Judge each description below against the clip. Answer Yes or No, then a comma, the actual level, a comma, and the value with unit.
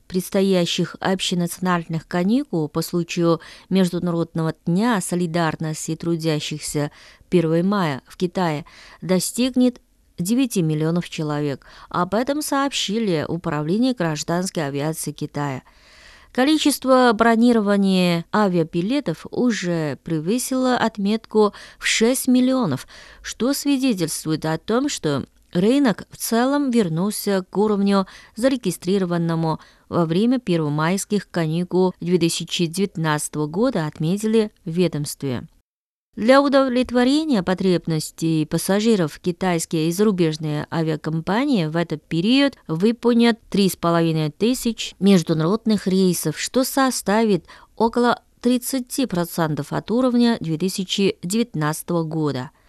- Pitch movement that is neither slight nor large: No, wide, 5.8 semitones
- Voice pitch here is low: No, medium, 185 Hz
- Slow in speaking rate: Yes, slow, 90 wpm